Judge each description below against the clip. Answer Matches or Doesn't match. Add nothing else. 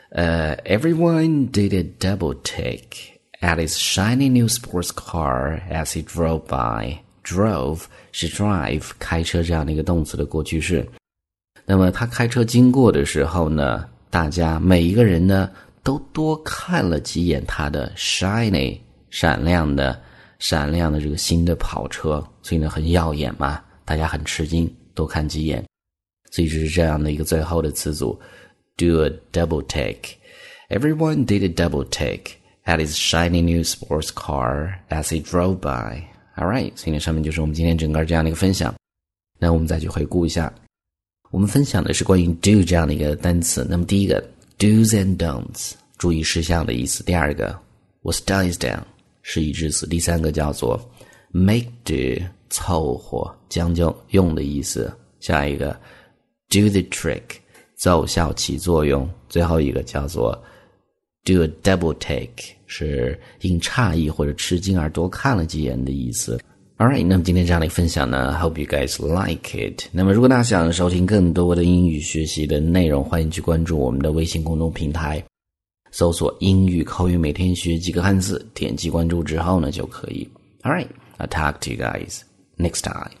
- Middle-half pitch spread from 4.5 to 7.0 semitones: Doesn't match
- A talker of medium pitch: Doesn't match